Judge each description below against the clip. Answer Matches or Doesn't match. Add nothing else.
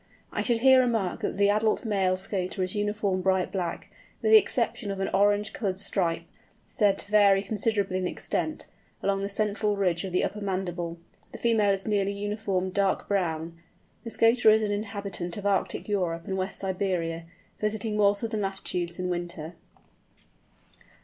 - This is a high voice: Matches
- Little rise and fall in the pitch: Matches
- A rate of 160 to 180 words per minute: Matches